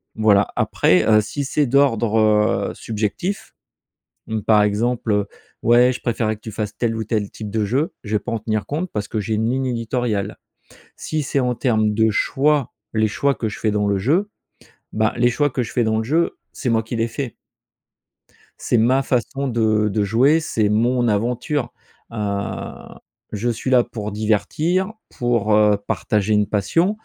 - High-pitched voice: No, low, 115 Hz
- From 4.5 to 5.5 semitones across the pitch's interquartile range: No, average, 3.1 semitones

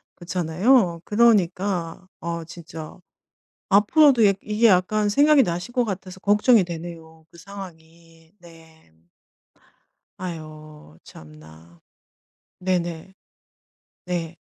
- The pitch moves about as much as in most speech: Yes, average, 3.8 semitones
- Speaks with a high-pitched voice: No, medium, 175 Hz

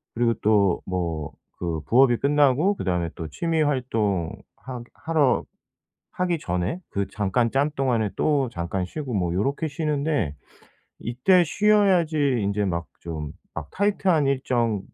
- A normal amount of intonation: No, wide, 8.2 semitones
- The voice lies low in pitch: Yes, low, 125 Hz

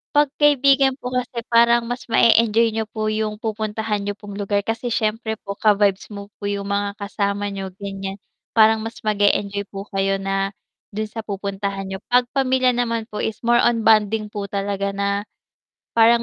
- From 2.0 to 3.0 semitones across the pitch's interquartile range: Yes, narrow, 2.4 semitones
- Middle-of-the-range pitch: No, high, 215 Hz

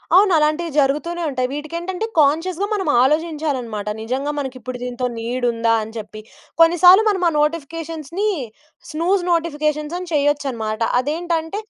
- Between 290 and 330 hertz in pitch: Yes, very high, 300 Hz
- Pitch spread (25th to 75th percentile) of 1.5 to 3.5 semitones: No, average, 4.9 semitones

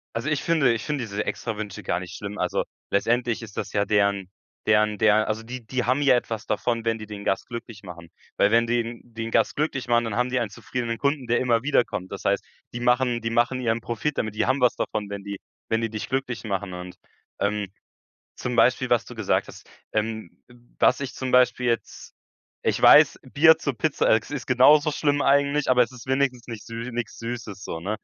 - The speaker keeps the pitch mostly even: No, average, 3.2 semitones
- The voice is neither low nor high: No, low, 115 Hz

